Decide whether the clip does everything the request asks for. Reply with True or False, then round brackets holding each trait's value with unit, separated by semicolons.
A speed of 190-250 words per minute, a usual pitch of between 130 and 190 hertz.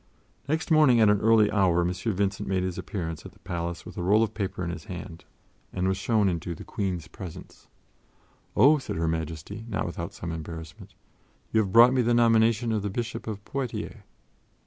False (195 wpm; 100 Hz)